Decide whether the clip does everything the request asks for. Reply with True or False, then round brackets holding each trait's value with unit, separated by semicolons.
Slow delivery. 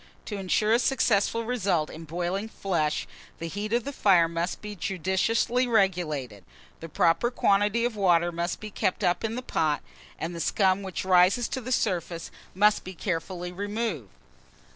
False (165 wpm)